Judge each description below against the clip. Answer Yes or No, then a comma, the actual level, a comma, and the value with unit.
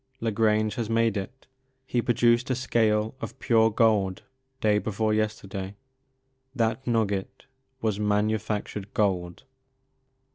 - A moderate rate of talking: No, slow, 115 wpm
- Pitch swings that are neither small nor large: No, narrow, 1.8 semitones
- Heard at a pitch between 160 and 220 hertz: No, low, 110 Hz